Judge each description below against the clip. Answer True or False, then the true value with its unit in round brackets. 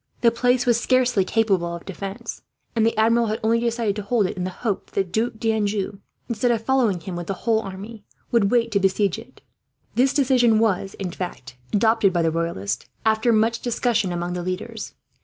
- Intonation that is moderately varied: True (3.6 semitones)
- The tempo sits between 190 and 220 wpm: True (200 wpm)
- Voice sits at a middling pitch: False (220 Hz)